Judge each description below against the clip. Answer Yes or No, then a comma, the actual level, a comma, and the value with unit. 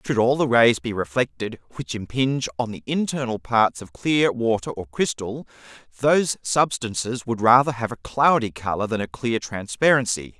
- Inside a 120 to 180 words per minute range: Yes, average, 165 wpm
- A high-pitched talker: No, low, 120 Hz